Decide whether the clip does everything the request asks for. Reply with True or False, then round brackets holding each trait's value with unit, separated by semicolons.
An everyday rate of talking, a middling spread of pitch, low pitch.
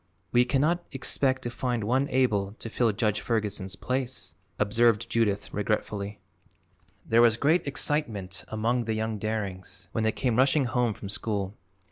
True (150 wpm; 3.4 semitones; 115 Hz)